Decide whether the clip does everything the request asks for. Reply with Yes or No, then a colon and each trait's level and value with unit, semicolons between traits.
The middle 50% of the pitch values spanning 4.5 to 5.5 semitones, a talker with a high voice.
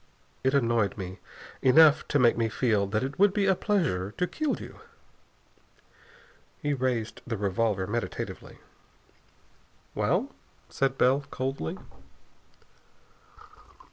No: average, 4.9 semitones; low, 125 Hz